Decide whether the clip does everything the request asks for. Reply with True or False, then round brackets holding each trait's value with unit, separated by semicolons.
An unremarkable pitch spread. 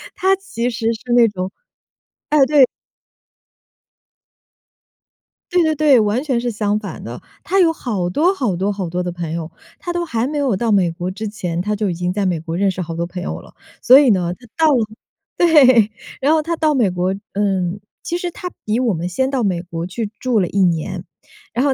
False (6.9 semitones)